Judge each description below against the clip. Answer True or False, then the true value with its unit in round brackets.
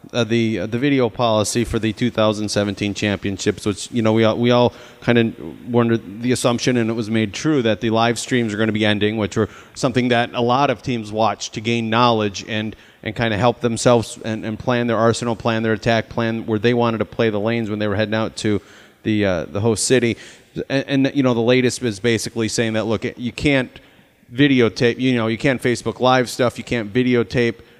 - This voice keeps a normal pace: False (230 wpm)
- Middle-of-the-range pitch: False (115 Hz)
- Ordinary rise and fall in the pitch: False (1.9 semitones)